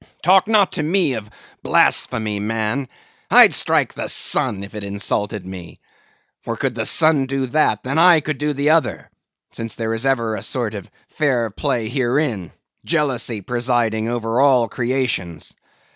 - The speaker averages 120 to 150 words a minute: No, average, 160 wpm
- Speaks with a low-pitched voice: Yes, low, 120 Hz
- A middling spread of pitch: Yes, average, 4.7 semitones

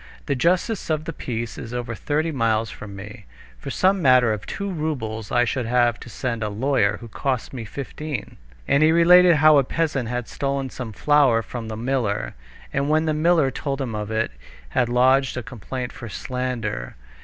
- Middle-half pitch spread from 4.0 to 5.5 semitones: Yes, average, 4.6 semitones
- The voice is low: Yes, low, 130 Hz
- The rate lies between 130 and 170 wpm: No, average, 190 wpm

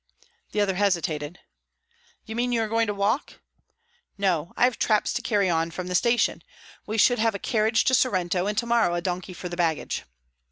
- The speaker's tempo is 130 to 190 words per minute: No, average, 200 wpm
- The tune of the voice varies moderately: Yes, average, 4.3 semitones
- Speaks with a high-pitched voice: Yes, high, 200 Hz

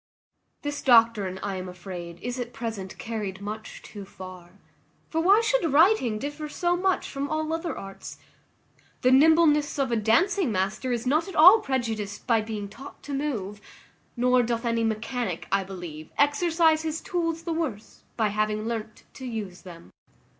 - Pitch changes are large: Yes, wide, 7.0 semitones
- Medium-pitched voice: No, high, 235 Hz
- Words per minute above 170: No, average, 165 wpm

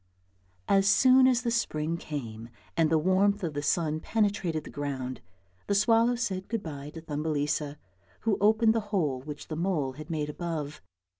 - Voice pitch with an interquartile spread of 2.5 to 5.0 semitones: No, wide, 5.6 semitones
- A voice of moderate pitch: Yes, medium, 165 Hz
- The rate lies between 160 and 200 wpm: Yes, average, 170 wpm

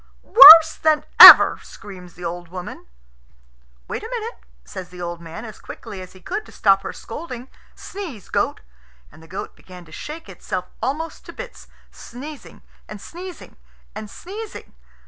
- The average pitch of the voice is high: Yes, high, 215 Hz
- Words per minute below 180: Yes, average, 160 wpm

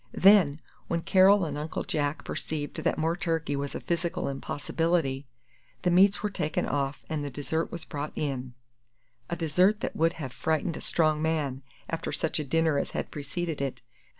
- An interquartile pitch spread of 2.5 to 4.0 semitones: Yes, average, 2.9 semitones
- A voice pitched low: No, medium, 160 Hz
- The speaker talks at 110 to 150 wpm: No, average, 180 wpm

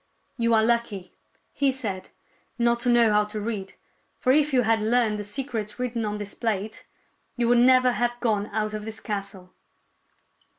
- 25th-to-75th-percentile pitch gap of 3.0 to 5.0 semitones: No, narrow, 2.5 semitones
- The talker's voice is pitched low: No, high, 225 Hz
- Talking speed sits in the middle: Yes, average, 185 wpm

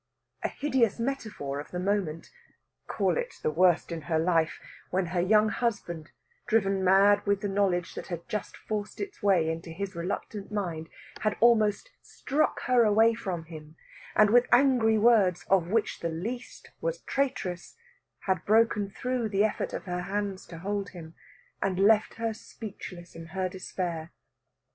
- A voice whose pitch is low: No, high, 195 Hz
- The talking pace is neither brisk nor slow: Yes, average, 160 wpm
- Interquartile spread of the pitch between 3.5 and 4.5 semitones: Yes, average, 4.1 semitones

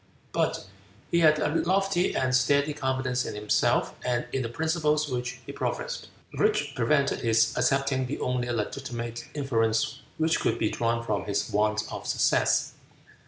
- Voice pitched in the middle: No, low, 125 Hz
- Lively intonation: No, average, 4.2 semitones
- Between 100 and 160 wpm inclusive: Yes, average, 155 wpm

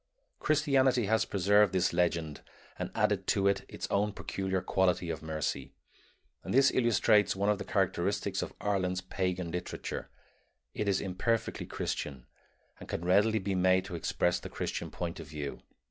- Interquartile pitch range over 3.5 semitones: No, average, 2.9 semitones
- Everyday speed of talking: Yes, average, 160 wpm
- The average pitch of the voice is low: Yes, very low, 95 Hz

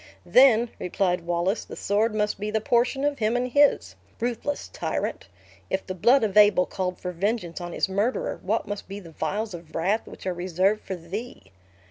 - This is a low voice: No, high, 205 Hz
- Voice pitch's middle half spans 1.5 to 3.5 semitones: No, average, 4.0 semitones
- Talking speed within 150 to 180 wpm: No, average, 190 wpm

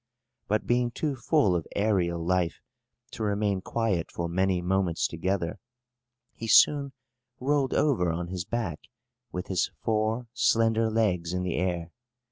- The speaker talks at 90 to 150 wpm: Yes, average, 140 wpm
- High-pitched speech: No, very low, 95 Hz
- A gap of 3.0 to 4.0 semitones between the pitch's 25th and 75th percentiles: No, average, 4.4 semitones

